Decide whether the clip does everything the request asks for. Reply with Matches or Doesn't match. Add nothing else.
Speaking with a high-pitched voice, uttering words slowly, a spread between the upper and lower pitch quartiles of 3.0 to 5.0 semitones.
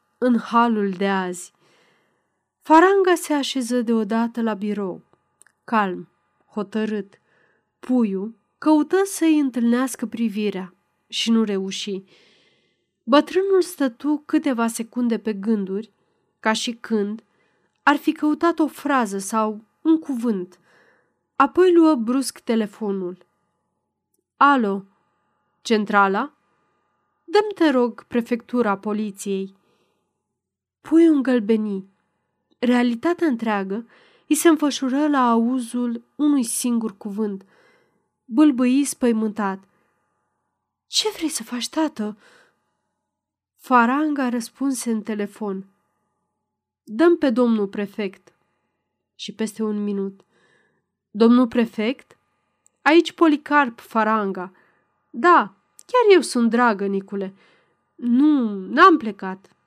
Doesn't match